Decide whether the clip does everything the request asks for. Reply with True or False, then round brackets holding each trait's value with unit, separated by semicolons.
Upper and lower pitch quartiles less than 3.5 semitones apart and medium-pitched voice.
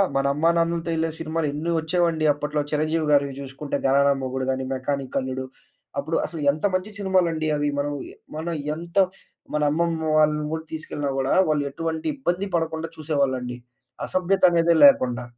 True (2.9 semitones; 155 Hz)